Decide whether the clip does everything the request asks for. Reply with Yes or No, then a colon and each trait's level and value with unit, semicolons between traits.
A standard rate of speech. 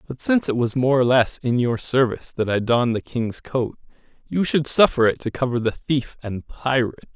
No: fast, 220 wpm